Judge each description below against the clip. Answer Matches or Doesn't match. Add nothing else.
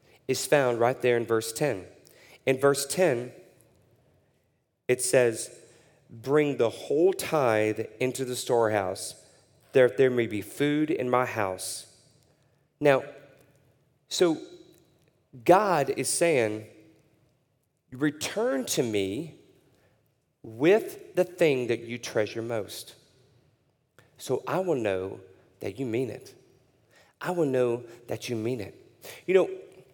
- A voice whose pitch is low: Matches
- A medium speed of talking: Doesn't match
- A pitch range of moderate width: Matches